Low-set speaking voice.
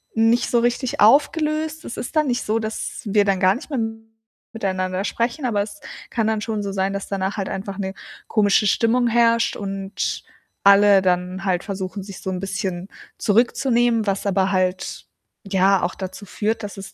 No: high, 205 Hz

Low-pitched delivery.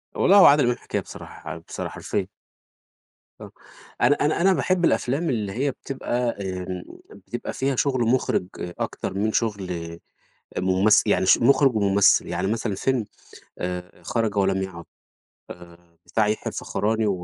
Yes: low, 105 Hz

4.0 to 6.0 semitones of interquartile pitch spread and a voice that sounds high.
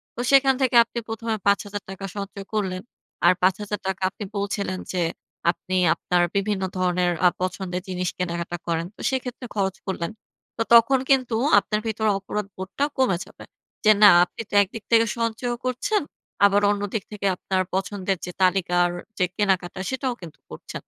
No: average, 3.4 semitones; high, 200 Hz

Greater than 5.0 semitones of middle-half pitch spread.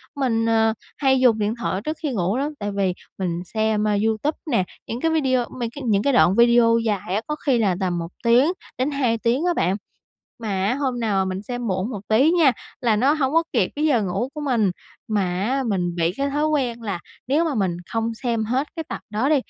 No: average, 4.7 semitones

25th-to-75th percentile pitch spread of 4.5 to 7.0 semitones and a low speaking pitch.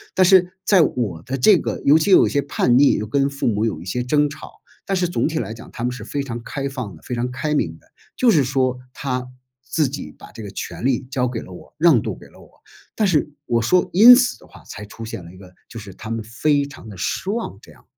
Yes: average, 5.2 semitones; low, 130 Hz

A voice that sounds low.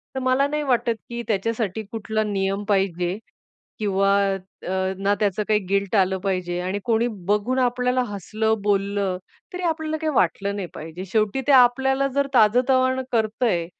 No: high, 215 Hz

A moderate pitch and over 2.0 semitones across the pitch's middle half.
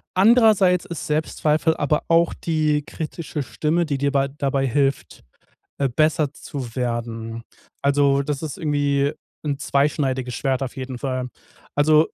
Yes: medium, 145 Hz; narrow, 2.4 semitones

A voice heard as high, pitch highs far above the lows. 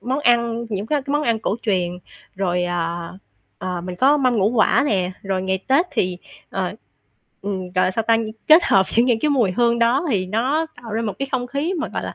Yes: high, 230 Hz; wide, 5.8 semitones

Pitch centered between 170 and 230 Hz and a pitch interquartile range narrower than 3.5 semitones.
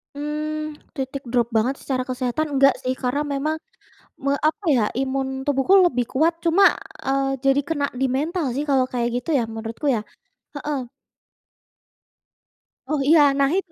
No: very high, 275 Hz; average, 3.1 semitones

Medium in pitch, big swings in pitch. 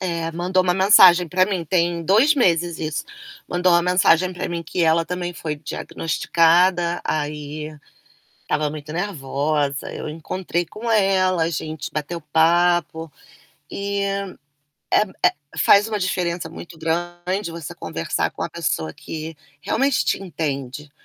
No: medium, 170 Hz; average, 2.8 semitones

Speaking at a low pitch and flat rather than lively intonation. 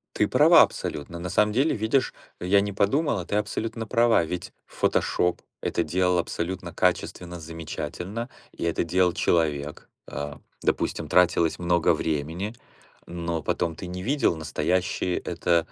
No: very low, 90 Hz; average, 3.2 semitones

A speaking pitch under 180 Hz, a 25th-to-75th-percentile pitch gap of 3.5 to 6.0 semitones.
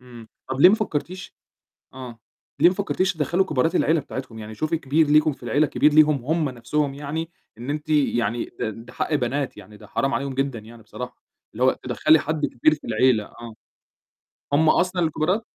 Yes: medium, 140 Hz; average, 4.2 semitones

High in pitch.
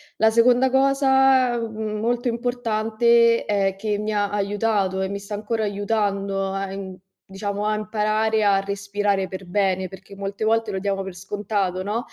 Yes: high, 205 Hz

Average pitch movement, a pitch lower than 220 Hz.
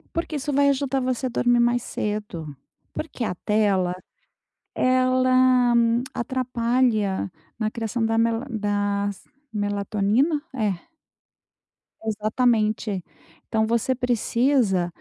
No: average, 3.6 semitones; high, 230 Hz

